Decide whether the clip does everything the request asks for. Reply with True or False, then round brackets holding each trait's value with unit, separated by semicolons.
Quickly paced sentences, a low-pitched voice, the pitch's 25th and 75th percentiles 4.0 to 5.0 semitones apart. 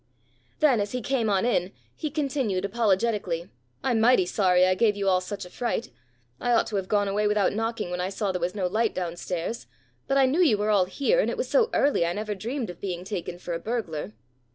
False (235 wpm; 205 Hz; 4.4 semitones)